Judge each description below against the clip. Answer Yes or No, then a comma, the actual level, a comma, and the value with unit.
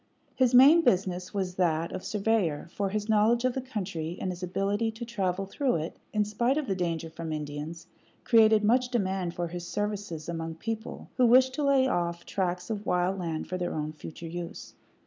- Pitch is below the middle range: No, high, 190 Hz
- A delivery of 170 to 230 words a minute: Yes, average, 195 wpm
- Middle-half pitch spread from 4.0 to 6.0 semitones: Yes, average, 4.7 semitones